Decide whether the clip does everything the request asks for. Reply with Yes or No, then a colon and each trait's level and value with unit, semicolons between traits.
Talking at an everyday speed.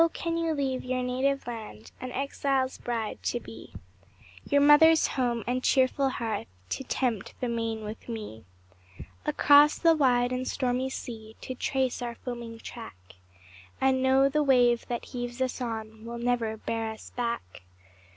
Yes: average, 155 wpm